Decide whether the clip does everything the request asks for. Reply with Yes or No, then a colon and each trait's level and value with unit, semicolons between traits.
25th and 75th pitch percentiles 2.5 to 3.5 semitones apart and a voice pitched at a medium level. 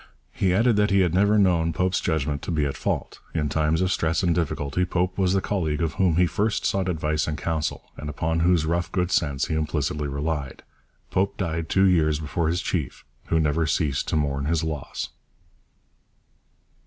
No: average, 3.1 semitones; very low, 80 Hz